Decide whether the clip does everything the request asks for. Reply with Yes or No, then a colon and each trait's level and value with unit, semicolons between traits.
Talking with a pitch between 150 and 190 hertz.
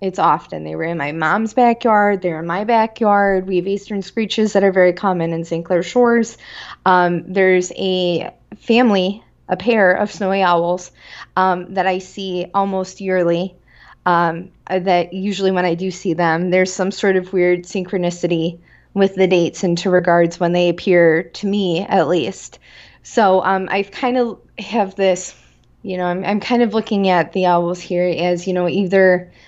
Yes: medium, 185 Hz